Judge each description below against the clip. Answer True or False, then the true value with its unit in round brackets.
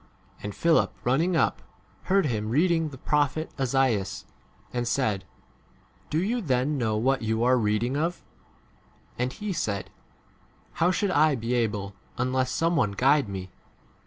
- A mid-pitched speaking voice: False (130 Hz)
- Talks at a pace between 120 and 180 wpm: True (150 wpm)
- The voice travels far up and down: True (5.9 semitones)